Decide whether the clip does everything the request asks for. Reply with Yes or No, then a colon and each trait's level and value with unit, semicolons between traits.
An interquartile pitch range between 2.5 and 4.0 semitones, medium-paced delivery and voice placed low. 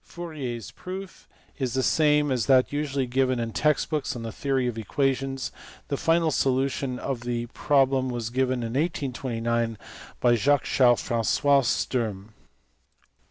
Yes: average, 2.9 semitones; average, 150 wpm; low, 130 Hz